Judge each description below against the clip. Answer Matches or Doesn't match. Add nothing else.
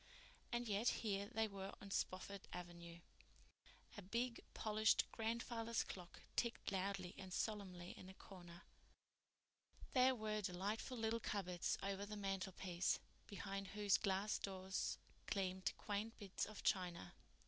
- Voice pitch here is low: Doesn't match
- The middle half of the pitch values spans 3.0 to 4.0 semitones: Doesn't match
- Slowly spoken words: Matches